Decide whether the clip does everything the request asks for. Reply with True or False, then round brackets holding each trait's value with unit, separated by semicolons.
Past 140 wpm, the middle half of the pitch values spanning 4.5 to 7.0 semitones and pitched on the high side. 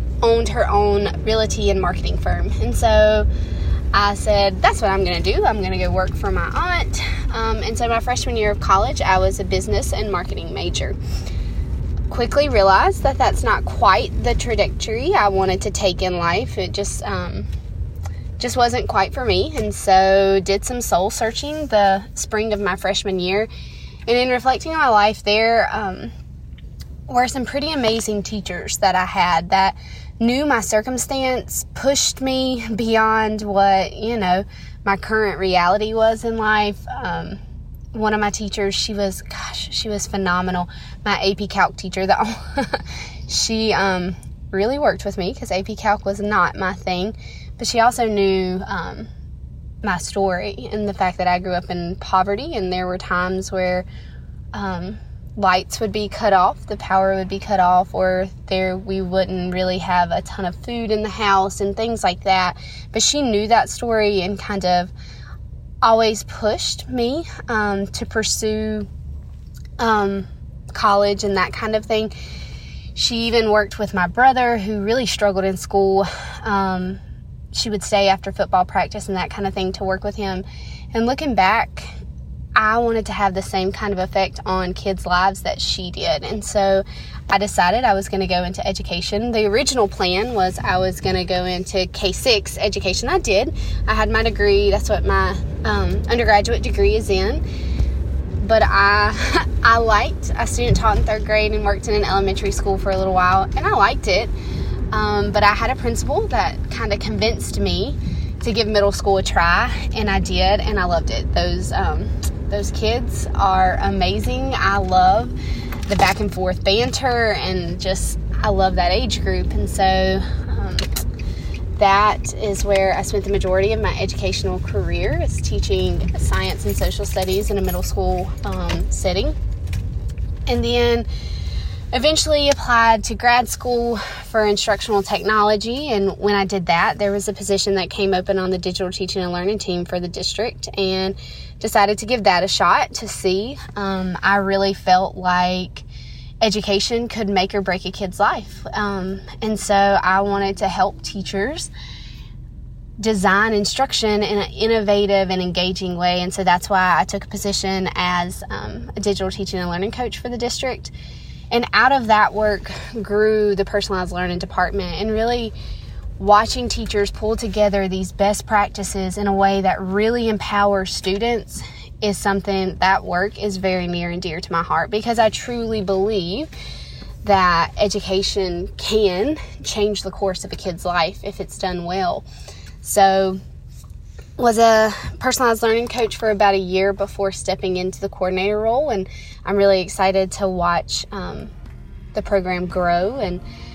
False (170 wpm; 2.8 semitones; 195 Hz)